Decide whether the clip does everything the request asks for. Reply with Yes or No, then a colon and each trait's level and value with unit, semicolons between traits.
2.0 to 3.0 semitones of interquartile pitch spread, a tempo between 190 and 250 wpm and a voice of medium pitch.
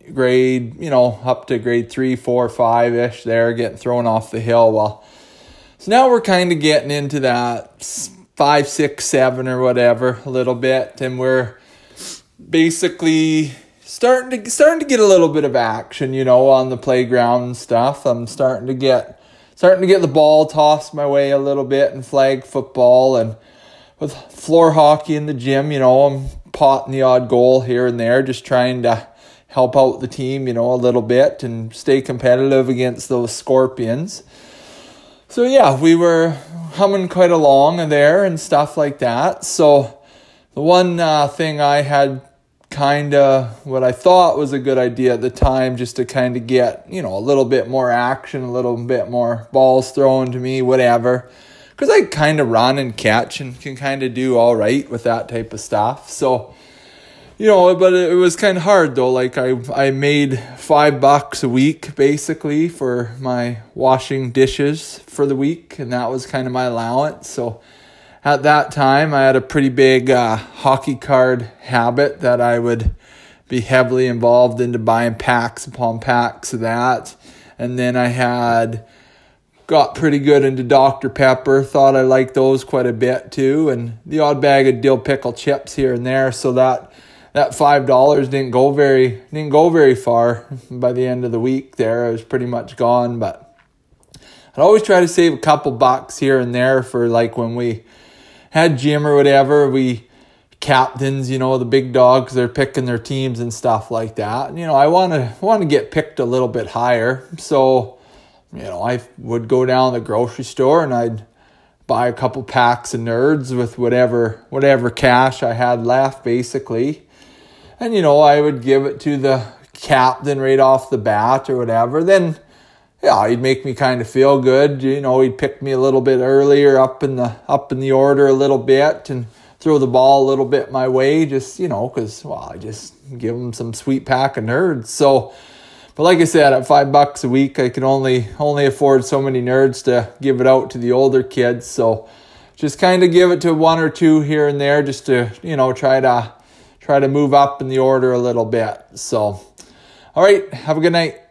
No: narrow, 2.6 semitones; average, 195 wpm; low, 130 Hz